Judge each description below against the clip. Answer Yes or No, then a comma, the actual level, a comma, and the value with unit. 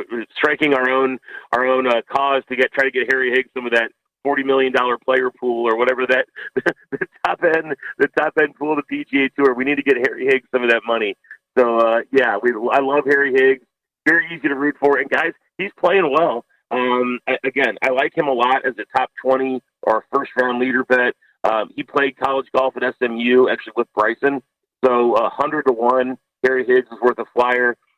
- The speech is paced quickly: Yes, fast, 215 wpm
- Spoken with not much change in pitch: Yes, narrow, 1.9 semitones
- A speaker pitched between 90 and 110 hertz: No, low, 130 Hz